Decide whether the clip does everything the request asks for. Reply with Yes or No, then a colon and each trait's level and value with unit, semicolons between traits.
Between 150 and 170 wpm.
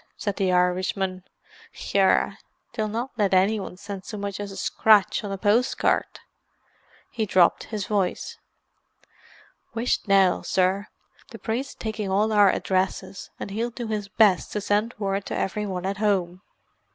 Yes: average, 155 wpm